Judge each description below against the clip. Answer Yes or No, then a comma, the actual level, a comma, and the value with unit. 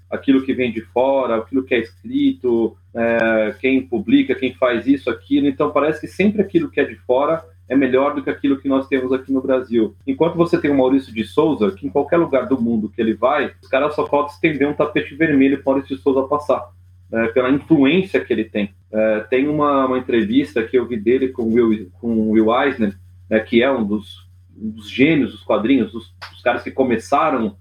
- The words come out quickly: Yes, fast, 220 wpm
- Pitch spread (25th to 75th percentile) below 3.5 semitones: No, average, 4.7 semitones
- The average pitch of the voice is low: Yes, low, 130 Hz